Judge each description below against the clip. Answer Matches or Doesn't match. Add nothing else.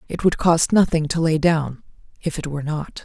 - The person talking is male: Doesn't match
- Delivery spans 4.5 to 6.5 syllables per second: Matches